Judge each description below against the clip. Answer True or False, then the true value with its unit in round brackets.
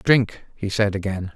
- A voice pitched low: True (105 Hz)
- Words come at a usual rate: True (180 wpm)